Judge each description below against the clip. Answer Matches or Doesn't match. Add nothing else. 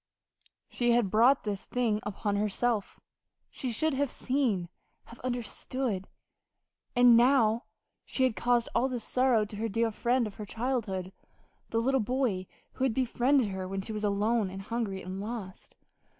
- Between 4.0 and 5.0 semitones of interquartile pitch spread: Doesn't match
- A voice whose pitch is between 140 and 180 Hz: Doesn't match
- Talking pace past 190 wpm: Doesn't match